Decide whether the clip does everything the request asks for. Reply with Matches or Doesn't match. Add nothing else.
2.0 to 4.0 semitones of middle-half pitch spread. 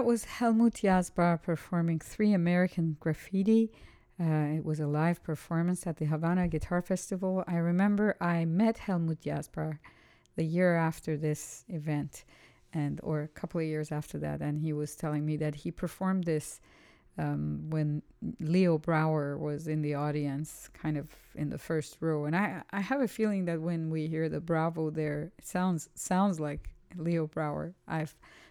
Matches